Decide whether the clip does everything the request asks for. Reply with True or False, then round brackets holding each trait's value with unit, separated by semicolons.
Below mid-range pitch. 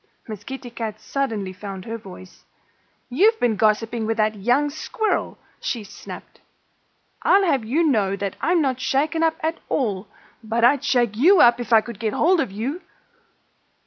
False (235 Hz)